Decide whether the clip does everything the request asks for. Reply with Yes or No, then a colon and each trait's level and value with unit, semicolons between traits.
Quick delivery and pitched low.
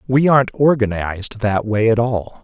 No: average, 175 wpm; low, 115 Hz